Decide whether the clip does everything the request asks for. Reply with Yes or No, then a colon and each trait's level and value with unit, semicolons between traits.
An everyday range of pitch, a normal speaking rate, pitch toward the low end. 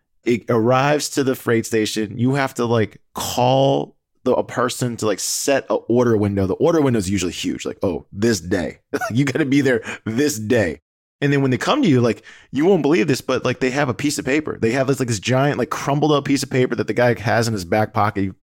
No: average, 3.8 semitones; fast, 250 wpm; low, 120 Hz